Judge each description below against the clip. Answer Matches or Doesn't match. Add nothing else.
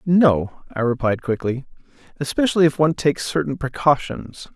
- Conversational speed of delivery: Doesn't match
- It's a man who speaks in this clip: Matches